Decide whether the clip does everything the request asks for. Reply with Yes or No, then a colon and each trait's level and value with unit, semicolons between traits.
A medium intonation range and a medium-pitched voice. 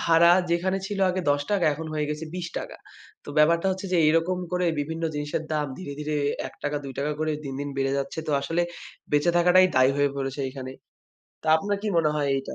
Yes: average, 3.4 semitones; medium, 155 Hz